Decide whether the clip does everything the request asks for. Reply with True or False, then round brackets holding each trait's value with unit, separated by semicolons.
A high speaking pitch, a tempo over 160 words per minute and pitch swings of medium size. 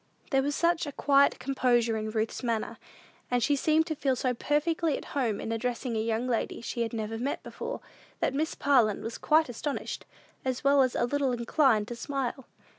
True (255 Hz; 195 wpm; 3.7 semitones)